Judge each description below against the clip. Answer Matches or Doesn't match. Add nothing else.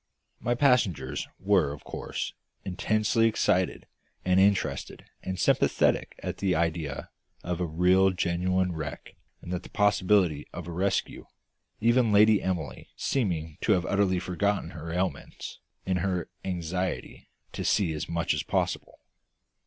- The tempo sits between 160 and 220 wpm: Doesn't match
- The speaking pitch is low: Matches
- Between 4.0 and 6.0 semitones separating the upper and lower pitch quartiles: Doesn't match